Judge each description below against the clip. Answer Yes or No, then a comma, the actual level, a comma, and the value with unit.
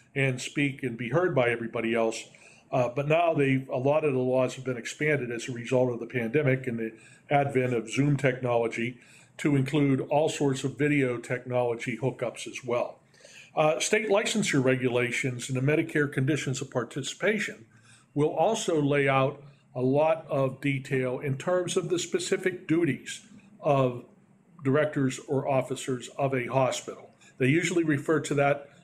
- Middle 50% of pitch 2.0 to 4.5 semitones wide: Yes, average, 3.3 semitones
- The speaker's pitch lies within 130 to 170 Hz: Yes, low, 135 Hz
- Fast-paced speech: No, average, 160 wpm